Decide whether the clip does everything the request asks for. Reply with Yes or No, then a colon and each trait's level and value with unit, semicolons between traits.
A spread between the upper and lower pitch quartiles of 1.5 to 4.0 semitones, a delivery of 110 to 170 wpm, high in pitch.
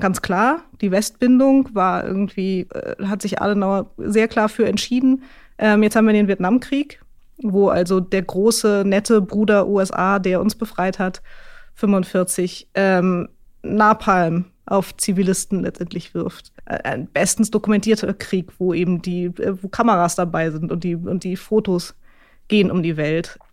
Yes: average, 2.9 semitones; average, 150 wpm; high, 195 Hz